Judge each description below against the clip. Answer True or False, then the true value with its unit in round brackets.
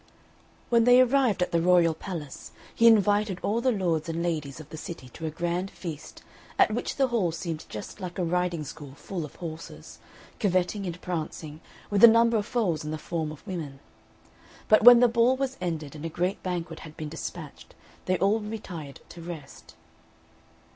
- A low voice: False (175 Hz)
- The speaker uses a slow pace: False (190 wpm)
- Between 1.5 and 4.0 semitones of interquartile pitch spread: False (4.8 semitones)